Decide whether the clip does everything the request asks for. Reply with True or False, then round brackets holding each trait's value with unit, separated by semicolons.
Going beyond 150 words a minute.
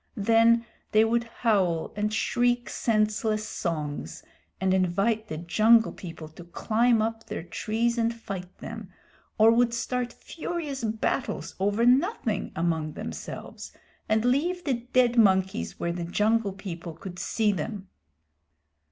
False (135 wpm)